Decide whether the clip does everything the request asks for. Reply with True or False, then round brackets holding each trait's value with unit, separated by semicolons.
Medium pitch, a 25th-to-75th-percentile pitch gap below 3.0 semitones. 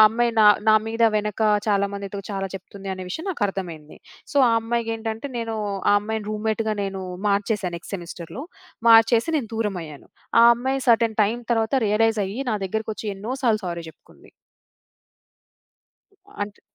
False (215 Hz; 2.5 semitones)